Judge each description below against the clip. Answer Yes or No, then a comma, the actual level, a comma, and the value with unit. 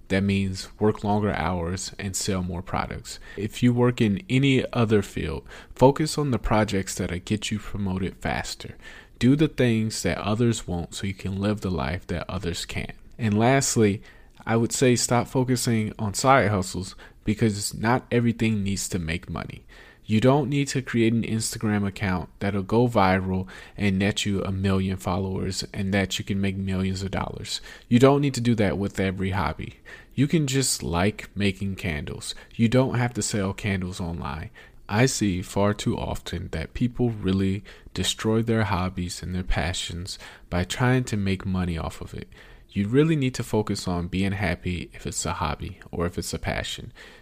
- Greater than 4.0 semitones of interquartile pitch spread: No, average, 3.6 semitones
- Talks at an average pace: Yes, average, 180 wpm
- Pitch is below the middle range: Yes, low, 100 Hz